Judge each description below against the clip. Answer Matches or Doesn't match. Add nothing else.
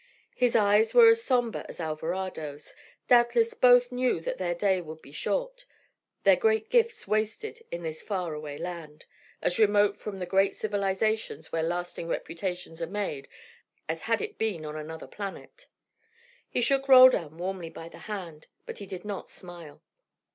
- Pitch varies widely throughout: Matches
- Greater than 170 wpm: Doesn't match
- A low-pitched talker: Doesn't match